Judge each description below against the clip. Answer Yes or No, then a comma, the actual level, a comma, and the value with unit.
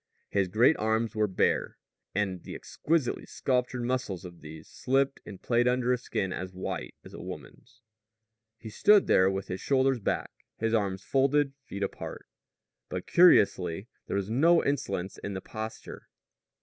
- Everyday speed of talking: Yes, average, 160 wpm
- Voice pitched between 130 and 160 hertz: No, low, 110 Hz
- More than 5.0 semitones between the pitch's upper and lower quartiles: Yes, wide, 5.4 semitones